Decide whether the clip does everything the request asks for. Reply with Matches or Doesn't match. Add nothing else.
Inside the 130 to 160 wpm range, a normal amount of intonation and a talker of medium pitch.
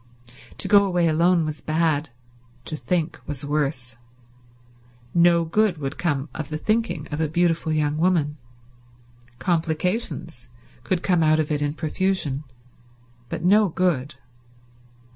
Matches